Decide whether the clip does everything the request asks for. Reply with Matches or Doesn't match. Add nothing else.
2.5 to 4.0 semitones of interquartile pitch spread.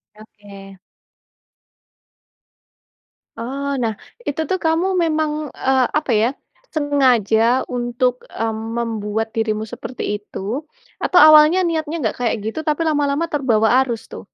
Doesn't match